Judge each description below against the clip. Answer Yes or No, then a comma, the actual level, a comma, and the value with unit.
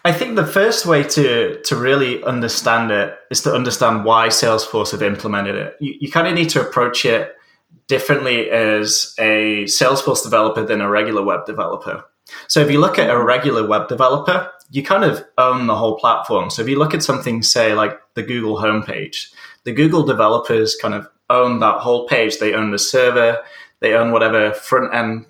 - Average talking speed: Yes, average, 190 wpm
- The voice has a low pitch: Yes, low, 125 Hz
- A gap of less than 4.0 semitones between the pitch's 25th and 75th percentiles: No, average, 4.7 semitones